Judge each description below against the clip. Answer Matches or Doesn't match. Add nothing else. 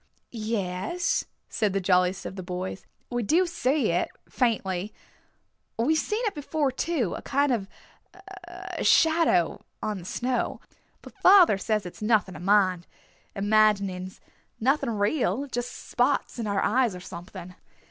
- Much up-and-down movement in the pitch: Matches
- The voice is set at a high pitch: Matches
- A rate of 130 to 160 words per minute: Matches